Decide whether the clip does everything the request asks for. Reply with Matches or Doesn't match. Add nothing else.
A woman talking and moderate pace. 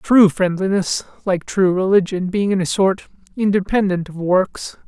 Doesn't match